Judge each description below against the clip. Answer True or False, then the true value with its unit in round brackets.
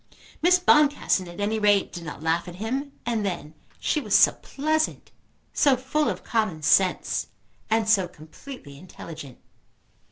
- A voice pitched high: True (210 Hz)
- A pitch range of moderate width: False (7.9 semitones)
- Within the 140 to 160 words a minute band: True (150 wpm)